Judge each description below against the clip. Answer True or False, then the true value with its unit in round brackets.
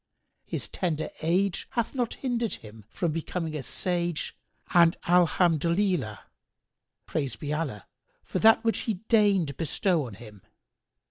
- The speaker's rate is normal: False (120 wpm)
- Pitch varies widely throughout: False (4.7 semitones)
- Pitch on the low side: False (170 Hz)